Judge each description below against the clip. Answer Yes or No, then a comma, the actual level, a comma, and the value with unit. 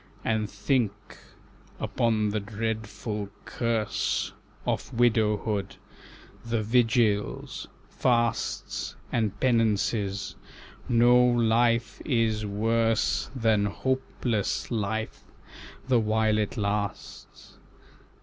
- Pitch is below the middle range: Yes, low, 110 Hz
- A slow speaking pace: Yes, slow, 80 wpm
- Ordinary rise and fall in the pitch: No, narrow, 1.9 semitones